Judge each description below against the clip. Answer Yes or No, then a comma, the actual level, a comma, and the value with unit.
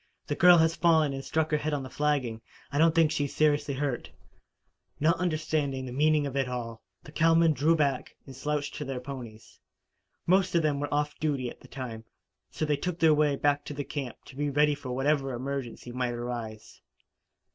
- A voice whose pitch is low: No, medium, 145 Hz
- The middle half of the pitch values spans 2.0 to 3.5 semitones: Yes, average, 2.8 semitones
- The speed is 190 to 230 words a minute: Yes, average, 200 wpm